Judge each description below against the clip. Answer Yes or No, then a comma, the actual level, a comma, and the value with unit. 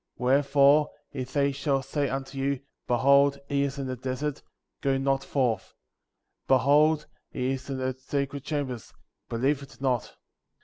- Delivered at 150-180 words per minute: Yes, average, 160 wpm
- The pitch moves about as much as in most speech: No, narrow, 1.4 semitones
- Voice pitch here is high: No, low, 135 Hz